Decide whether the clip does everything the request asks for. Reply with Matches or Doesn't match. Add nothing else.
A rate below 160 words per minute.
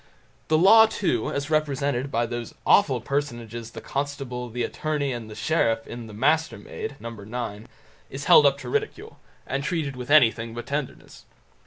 Doesn't match